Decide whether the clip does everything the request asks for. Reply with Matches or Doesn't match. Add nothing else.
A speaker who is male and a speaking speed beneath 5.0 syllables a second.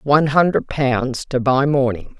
Doesn't match